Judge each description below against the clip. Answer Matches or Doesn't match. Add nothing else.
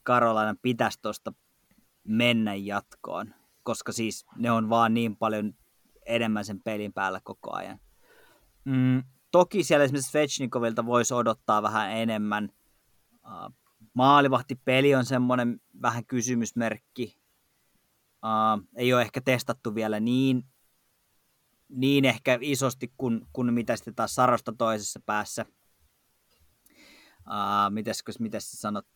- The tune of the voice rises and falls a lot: Doesn't match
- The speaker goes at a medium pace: Matches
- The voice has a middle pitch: Doesn't match